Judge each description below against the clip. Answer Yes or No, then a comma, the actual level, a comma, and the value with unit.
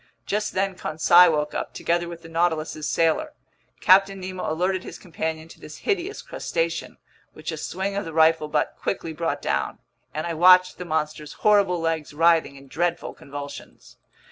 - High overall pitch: No, medium, 165 Hz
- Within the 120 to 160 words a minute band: No, average, 170 wpm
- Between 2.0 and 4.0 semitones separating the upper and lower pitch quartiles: Yes, average, 3.0 semitones